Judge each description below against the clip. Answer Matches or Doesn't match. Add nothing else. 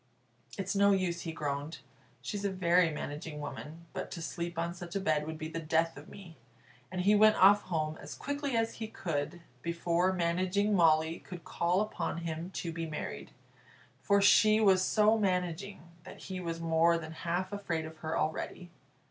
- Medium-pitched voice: Matches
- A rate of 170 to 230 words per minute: Matches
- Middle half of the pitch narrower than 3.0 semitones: Doesn't match